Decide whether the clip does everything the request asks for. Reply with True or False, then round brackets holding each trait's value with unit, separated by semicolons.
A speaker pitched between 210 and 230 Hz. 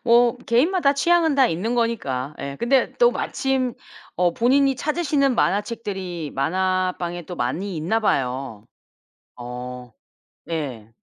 False (190 Hz)